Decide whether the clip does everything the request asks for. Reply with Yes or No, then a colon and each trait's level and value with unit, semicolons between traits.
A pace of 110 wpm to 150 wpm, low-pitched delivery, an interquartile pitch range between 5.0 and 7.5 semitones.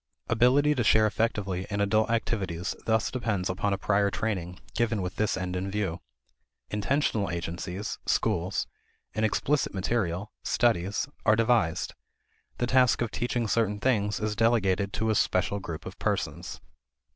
No: average, 145 wpm; low, 105 Hz; average, 3.5 semitones